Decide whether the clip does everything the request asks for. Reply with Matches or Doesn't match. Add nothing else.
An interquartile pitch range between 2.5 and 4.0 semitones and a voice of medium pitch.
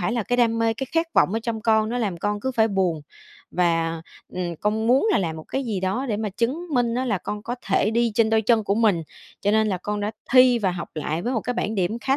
Doesn't match